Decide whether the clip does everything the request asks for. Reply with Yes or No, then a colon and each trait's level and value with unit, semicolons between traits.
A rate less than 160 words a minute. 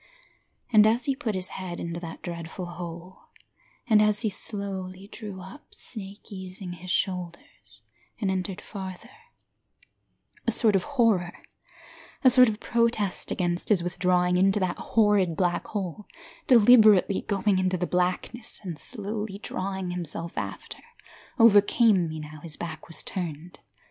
Yes: average, 140 wpm